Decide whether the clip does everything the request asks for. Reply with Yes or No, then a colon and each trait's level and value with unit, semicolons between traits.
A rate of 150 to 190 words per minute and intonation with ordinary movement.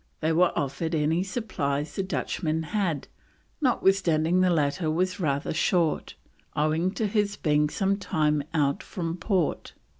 No: average, 140 wpm; average, 3.8 semitones